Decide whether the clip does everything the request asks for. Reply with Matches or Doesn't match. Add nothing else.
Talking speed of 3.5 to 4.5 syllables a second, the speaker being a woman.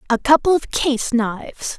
Matches